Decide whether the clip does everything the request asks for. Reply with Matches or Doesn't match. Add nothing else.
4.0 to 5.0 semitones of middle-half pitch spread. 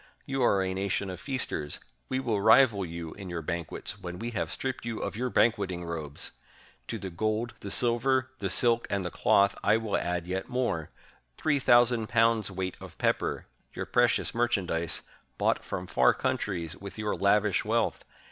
Matches